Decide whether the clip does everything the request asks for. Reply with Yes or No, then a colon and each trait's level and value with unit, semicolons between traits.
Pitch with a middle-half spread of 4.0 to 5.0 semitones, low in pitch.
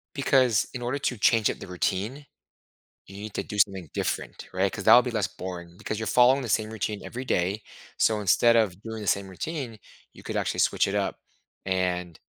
Yes: average, 4.4 semitones; low, 105 Hz